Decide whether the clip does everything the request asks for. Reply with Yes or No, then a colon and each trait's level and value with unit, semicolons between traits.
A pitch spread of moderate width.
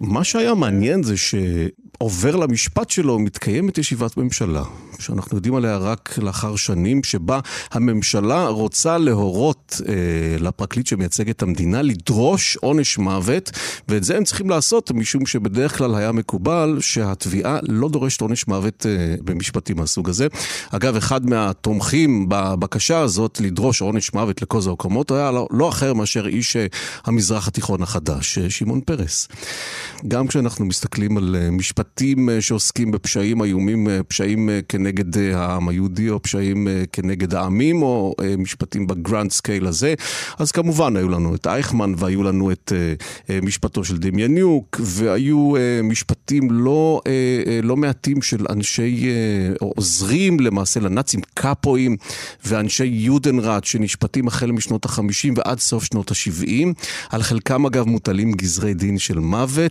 Yes: average, 4.6 semitones